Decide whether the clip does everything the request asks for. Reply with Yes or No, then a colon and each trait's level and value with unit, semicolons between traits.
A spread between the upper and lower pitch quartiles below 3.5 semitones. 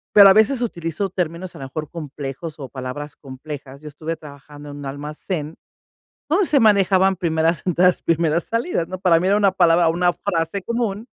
No: average, 4.4 semitones